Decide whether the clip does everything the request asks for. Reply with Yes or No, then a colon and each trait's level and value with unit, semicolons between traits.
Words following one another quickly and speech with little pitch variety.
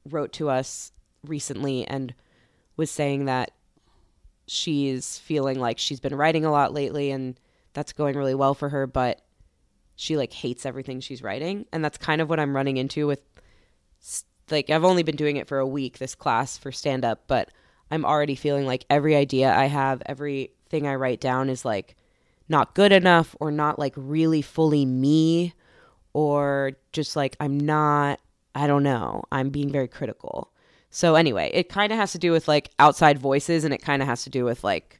No: average, 190 wpm; narrow, 2.3 semitones